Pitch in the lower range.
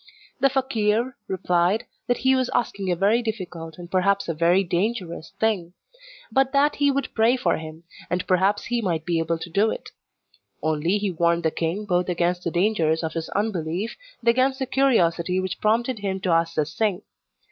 No: high, 190 Hz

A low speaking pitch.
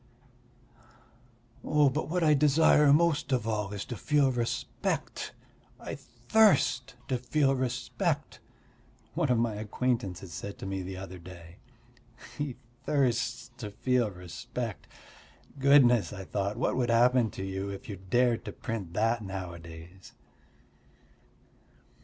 Yes: low, 120 Hz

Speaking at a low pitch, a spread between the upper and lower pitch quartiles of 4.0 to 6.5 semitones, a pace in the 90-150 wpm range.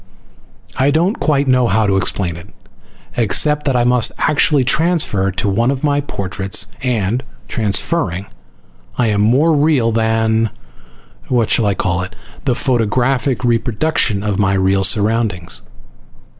Yes: low, 115 Hz; average, 5.1 semitones; average, 140 wpm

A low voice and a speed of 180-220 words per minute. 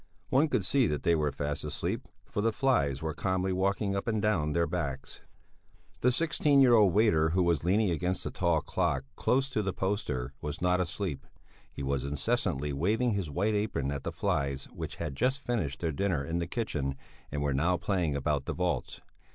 Yes: very low, 85 Hz; average, 200 wpm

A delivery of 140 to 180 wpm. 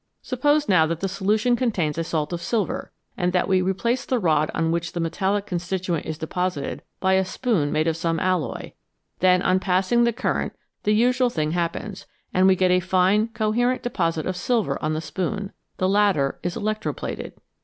No: average, 190 wpm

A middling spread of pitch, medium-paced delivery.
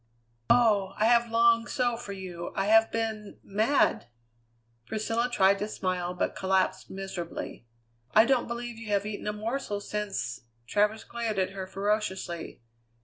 Yes: average, 3.1 semitones; average, 150 wpm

